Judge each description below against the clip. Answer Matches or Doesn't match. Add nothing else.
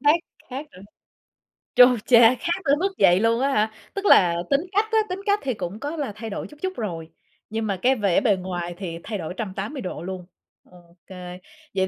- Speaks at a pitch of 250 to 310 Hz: Doesn't match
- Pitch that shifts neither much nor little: Doesn't match